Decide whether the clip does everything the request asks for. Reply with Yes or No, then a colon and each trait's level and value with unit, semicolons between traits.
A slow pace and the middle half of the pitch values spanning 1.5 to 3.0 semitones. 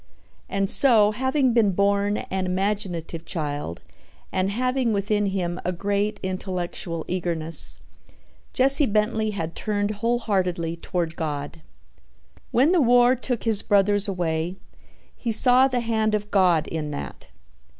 No: slow, 130 wpm; average, 4.3 semitones